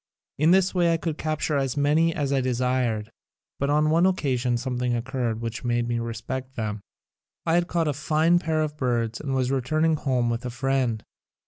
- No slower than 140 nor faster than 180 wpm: No, average, 195 wpm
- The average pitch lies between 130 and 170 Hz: Yes, low, 135 Hz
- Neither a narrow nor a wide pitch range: Yes, average, 4.3 semitones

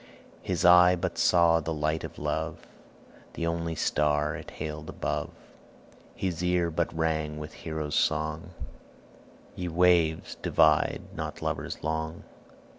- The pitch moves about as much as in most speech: No, narrow, 1.8 semitones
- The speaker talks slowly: Yes, slow, 125 wpm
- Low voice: Yes, very low, 80 Hz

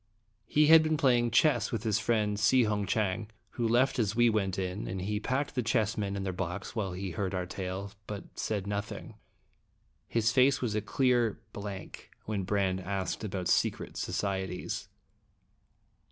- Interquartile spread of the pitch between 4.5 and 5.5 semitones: No, average, 3.3 semitones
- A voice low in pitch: Yes, low, 105 Hz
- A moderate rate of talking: Yes, average, 170 wpm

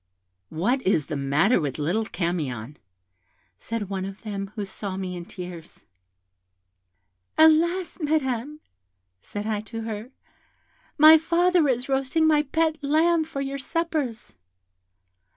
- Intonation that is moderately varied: No, wide, 8.6 semitones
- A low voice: No, high, 230 Hz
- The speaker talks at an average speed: No, slow, 125 wpm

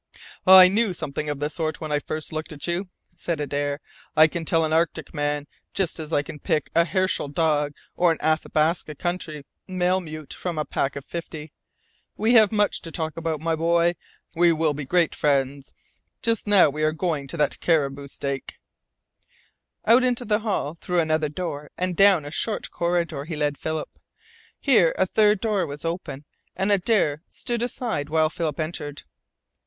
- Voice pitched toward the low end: No, medium, 160 Hz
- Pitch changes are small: No, average, 3.5 semitones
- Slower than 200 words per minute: Yes, average, 180 wpm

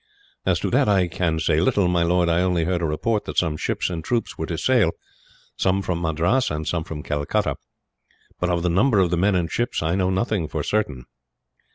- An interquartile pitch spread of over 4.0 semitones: No, average, 3.0 semitones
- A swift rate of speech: Yes, fast, 220 wpm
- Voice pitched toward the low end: Yes, very low, 90 Hz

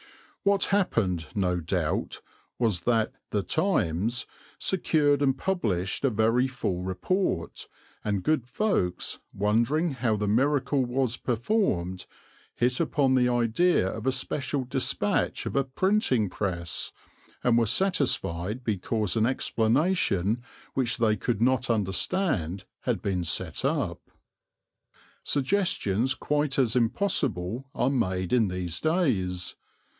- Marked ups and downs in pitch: Yes, wide, 6.2 semitones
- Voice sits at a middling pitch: No, low, 120 Hz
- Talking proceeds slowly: Yes, slow, 120 wpm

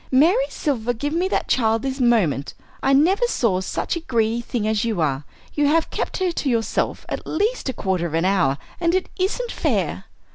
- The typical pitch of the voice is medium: No, very high, 250 Hz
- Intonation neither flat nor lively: No, wide, 7.9 semitones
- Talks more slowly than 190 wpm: No, fast, 205 wpm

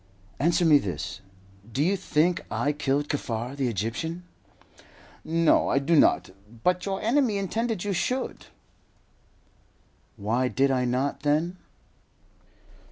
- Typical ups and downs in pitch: No, wide, 5.8 semitones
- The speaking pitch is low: No, medium, 150 Hz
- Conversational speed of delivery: No, slow, 120 wpm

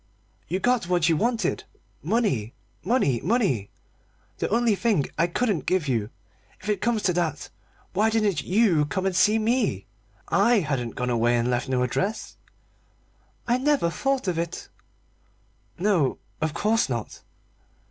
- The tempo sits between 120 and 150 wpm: Yes, average, 145 wpm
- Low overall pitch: No, medium, 185 Hz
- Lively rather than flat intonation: Yes, wide, 7.6 semitones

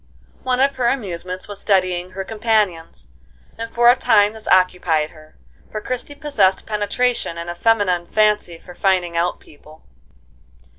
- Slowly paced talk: No, average, 150 wpm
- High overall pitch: Yes, high, 195 Hz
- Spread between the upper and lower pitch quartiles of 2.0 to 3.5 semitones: No, average, 4.4 semitones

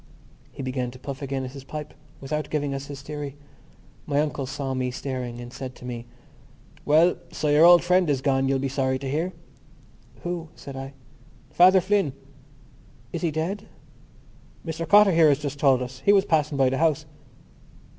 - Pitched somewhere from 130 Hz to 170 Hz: Yes, medium, 140 Hz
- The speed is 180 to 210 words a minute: Yes, average, 185 wpm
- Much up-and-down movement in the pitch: No, average, 3.3 semitones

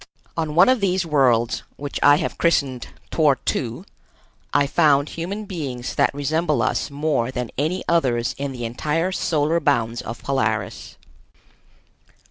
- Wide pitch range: No, average, 4.8 semitones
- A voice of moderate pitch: Yes, medium, 145 Hz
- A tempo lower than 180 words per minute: Yes, average, 140 wpm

